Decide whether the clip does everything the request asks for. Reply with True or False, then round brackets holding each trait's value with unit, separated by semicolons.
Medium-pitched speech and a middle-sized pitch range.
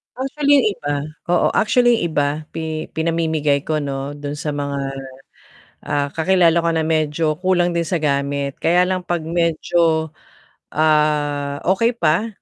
True (160 Hz; 3.0 semitones)